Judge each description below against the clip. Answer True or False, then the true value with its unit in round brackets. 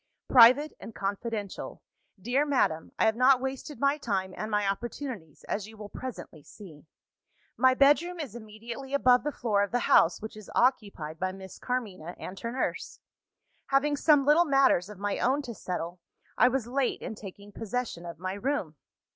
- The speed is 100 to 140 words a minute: False (175 wpm)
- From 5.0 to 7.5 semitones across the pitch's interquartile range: True (5.3 semitones)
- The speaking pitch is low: False (230 Hz)